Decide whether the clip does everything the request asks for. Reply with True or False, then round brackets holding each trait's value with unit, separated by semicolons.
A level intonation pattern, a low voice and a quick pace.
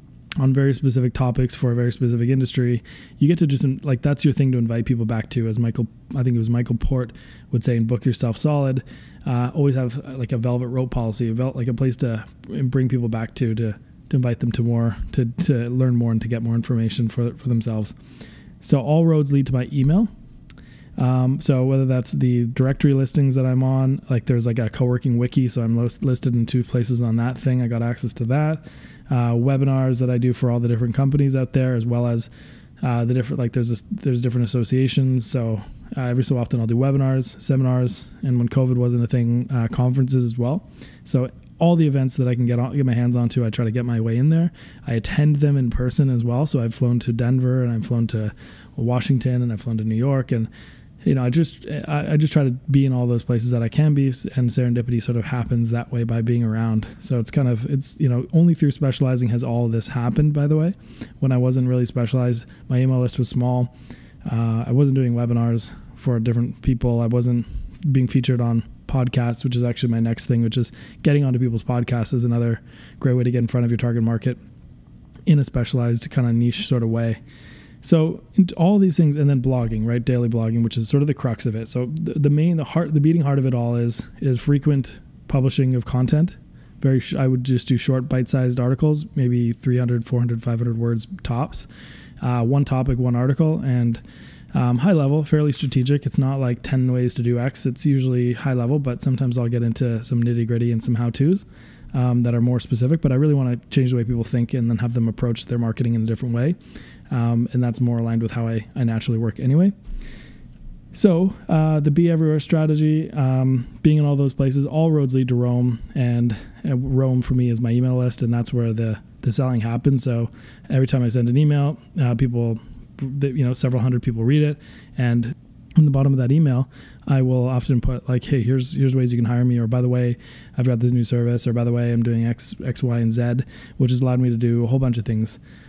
True (2.1 semitones; 125 Hz; 230 wpm)